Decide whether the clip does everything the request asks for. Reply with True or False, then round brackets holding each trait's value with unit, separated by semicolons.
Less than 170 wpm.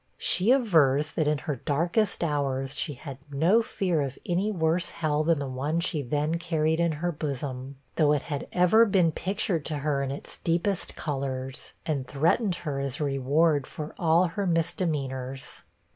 False (175 wpm)